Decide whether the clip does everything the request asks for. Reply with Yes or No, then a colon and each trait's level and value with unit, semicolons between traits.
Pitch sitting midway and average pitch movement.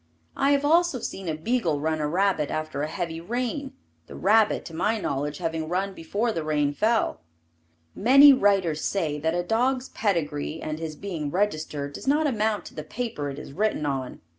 No: medium, 175 Hz; wide, 6.5 semitones